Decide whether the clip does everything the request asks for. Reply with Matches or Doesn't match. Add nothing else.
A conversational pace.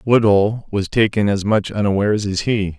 Matches